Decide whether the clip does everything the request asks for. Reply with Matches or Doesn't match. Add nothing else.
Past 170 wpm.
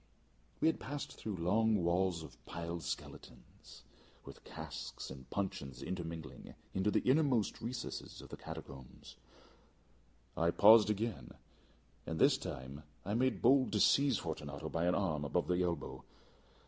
Doesn't match